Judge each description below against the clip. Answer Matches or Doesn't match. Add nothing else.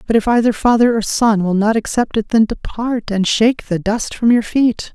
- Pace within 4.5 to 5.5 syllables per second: Matches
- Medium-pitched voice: Doesn't match